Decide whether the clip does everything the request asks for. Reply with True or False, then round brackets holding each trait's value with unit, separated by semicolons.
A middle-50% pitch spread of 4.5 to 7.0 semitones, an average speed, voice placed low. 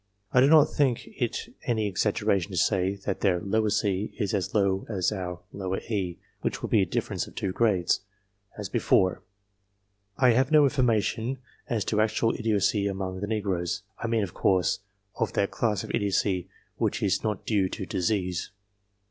False (3.3 semitones; 170 wpm; 100 Hz)